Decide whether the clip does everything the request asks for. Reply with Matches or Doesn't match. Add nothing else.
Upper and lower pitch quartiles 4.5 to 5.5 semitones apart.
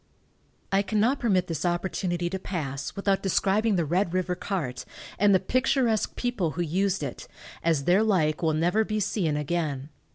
Doesn't match